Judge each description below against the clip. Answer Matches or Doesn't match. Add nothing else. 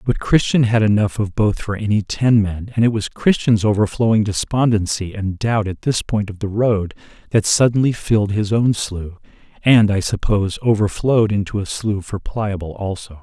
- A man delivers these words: Matches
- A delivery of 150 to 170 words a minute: Doesn't match